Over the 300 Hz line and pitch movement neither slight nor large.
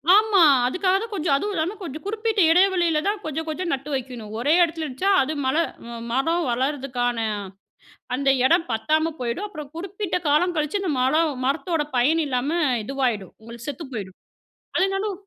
No: very high, 310 Hz; wide, 5.8 semitones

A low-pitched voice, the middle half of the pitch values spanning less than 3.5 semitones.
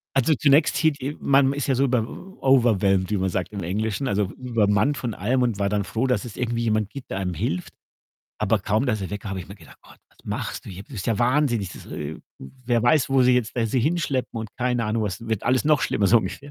No: low, 115 Hz; average, 4.4 semitones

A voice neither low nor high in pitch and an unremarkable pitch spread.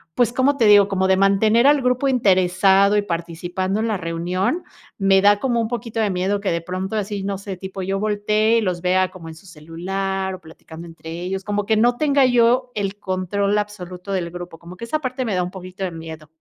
No: high, 195 Hz; average, 3.1 semitones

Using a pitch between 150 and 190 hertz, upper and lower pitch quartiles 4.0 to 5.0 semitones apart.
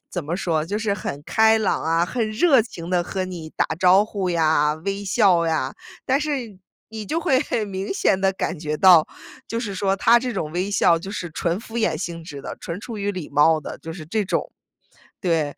Yes: medium, 185 Hz; average, 4.5 semitones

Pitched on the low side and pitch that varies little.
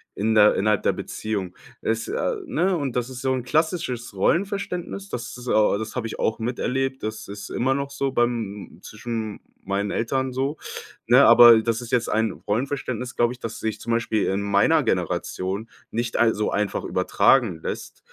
No: low, 115 Hz; average, 3.5 semitones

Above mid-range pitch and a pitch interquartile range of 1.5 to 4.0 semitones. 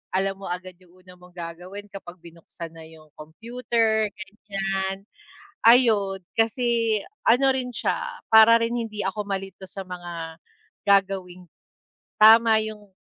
Yes: high, 195 Hz; average, 3.7 semitones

